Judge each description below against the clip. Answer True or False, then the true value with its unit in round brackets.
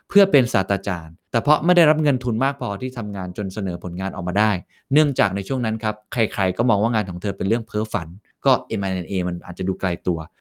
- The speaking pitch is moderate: False (105 Hz)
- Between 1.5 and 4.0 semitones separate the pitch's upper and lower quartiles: False (4.5 semitones)